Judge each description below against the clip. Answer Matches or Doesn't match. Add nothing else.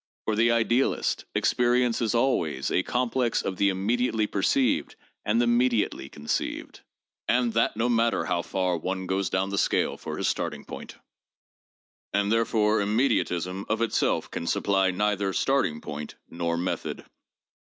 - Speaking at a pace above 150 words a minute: Doesn't match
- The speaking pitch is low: Matches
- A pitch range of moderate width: Matches